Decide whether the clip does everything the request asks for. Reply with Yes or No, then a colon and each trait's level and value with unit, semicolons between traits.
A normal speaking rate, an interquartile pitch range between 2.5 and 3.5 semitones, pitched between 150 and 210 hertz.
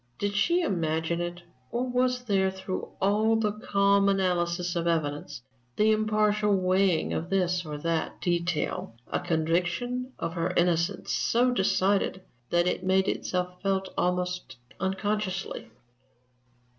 No: slow, 130 wpm; average, 3.1 semitones; high, 190 Hz